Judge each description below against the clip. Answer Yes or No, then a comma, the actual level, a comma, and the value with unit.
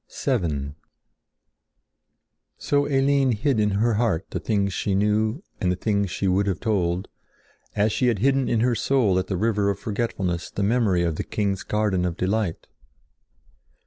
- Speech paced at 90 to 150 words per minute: No, average, 165 wpm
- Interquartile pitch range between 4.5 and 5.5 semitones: No, average, 3.8 semitones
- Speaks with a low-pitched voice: Yes, low, 105 Hz